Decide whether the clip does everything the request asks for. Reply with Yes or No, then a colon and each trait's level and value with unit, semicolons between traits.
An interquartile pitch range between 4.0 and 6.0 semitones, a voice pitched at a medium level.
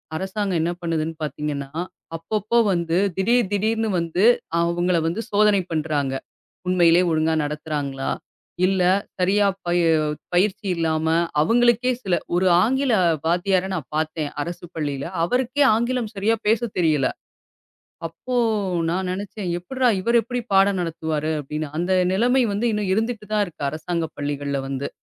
Yes: average, 5.1 semitones; medium, 180 Hz